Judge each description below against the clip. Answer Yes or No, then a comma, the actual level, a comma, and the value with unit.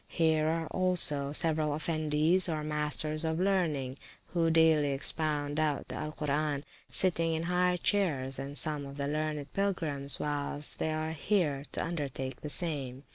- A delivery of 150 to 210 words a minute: Yes, average, 155 wpm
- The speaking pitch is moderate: Yes, medium, 155 Hz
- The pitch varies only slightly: Yes, narrow, 2.2 semitones